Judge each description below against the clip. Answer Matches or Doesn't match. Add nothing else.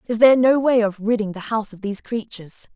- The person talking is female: Matches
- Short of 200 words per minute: Doesn't match